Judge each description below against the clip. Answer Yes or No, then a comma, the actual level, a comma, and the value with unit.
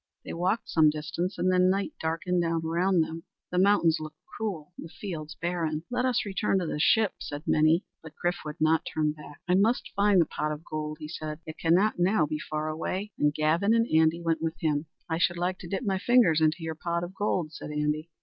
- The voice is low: No, medium, 165 Hz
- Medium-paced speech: No, fast, 225 wpm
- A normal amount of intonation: Yes, average, 3.2 semitones